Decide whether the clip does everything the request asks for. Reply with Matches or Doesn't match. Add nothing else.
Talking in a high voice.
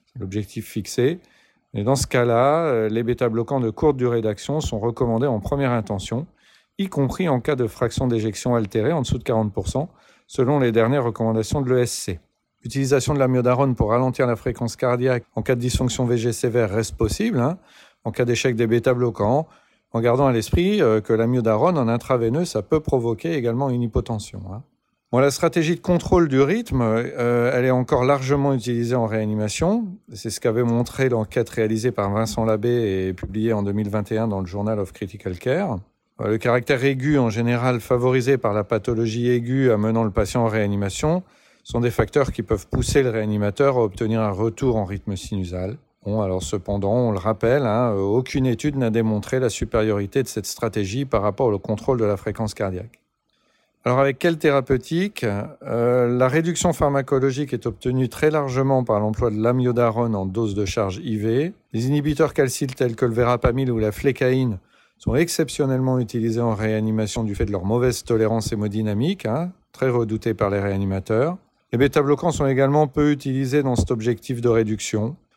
Doesn't match